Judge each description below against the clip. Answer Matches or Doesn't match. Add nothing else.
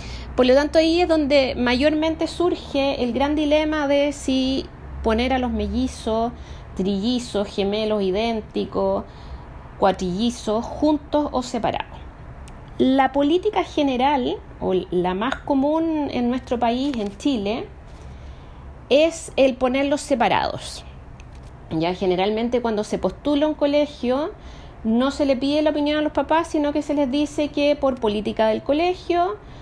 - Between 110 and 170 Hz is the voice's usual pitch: Doesn't match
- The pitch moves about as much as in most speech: Doesn't match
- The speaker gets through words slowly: Doesn't match